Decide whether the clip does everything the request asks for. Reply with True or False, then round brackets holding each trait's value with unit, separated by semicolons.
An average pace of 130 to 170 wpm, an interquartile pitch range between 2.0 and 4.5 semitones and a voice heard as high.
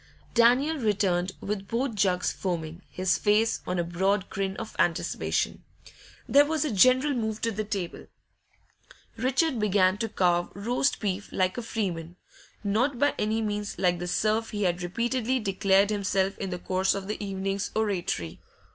True (160 wpm; 3.4 semitones; 200 Hz)